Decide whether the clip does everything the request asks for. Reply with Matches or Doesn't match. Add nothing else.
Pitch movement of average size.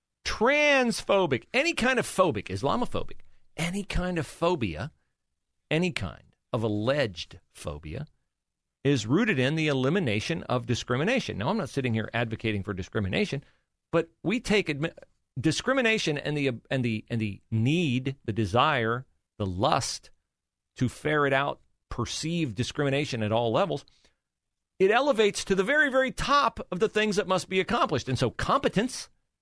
Doesn't match